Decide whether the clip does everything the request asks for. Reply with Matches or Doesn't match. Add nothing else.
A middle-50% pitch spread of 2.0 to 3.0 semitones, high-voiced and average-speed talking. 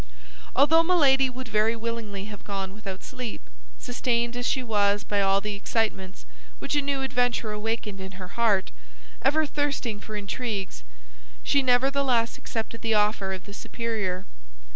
Doesn't match